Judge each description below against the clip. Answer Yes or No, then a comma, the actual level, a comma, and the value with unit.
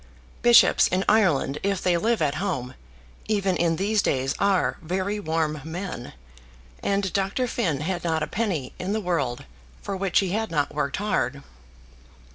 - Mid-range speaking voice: Yes, medium, 180 Hz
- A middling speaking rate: Yes, average, 160 wpm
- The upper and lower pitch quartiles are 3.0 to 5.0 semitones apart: Yes, average, 4.6 semitones